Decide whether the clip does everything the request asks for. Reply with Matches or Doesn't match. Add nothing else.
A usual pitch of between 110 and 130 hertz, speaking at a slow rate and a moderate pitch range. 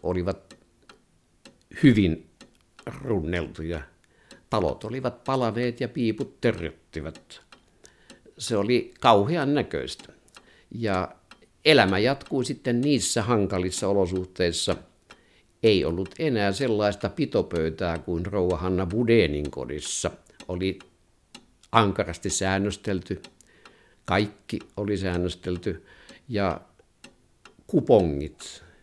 Doesn't match